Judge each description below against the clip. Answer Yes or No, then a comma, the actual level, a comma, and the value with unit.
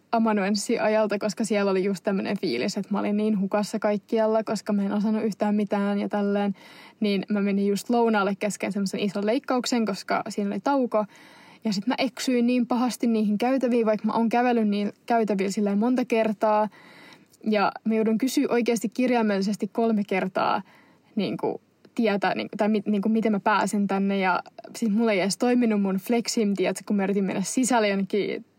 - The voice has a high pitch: Yes, high, 215 Hz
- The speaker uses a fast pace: Yes, fast, 185 wpm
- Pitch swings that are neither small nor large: No, narrow, 2.2 semitones